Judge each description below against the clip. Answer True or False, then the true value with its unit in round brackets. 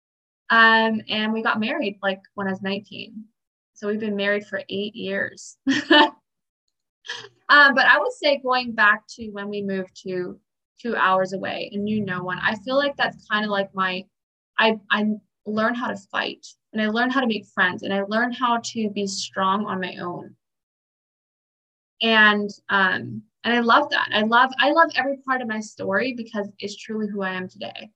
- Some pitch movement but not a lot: True (3.0 semitones)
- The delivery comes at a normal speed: True (190 wpm)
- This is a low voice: False (215 Hz)